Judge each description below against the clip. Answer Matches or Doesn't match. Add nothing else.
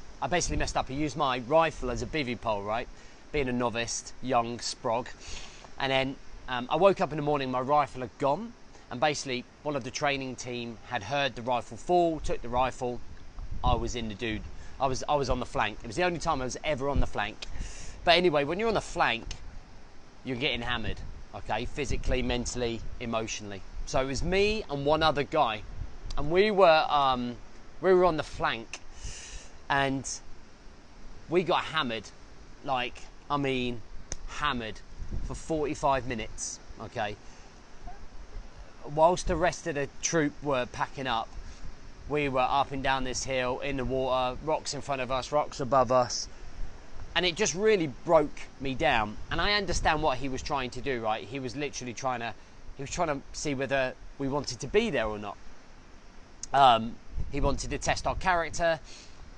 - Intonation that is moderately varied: Matches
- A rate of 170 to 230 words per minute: Matches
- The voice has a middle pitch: Doesn't match